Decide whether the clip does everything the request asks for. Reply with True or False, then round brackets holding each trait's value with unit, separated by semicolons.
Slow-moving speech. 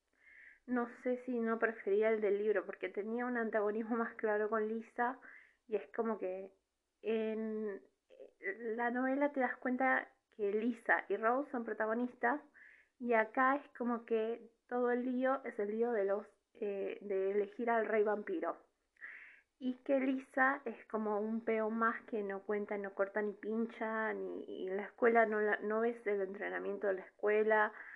False (170 wpm)